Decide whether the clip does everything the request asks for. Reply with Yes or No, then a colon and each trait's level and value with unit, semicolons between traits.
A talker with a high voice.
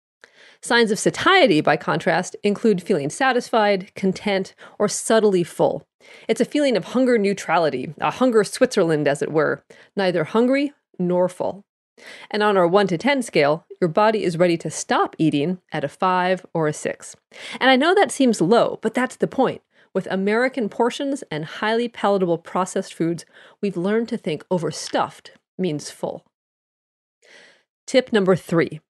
Yes: high, 200 Hz